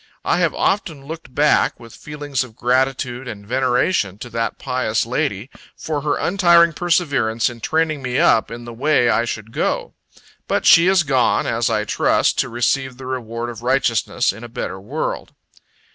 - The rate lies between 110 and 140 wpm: No, average, 175 wpm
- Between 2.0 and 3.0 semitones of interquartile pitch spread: No, average, 4.2 semitones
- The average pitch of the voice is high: No, low, 130 Hz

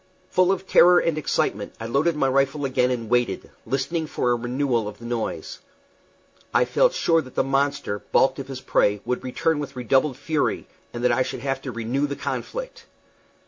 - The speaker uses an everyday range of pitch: Yes, average, 3.4 semitones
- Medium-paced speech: Yes, average, 190 wpm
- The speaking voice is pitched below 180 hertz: Yes, low, 135 Hz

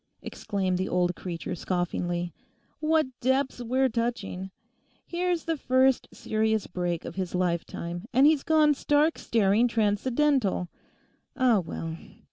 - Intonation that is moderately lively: No, wide, 6.8 semitones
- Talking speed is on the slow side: Yes, slow, 120 wpm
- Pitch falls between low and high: No, high, 220 Hz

